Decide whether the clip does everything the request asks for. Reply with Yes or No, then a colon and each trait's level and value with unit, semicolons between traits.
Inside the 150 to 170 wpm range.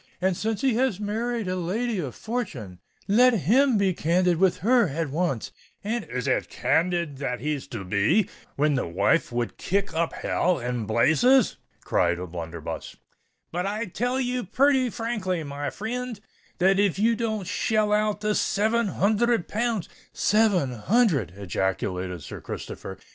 Yes: average, 155 wpm